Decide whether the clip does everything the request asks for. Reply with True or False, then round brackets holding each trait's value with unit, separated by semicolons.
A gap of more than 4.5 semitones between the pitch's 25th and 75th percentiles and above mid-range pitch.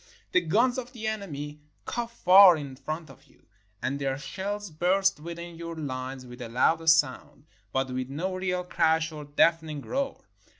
False (5.0 semitones; 160 Hz)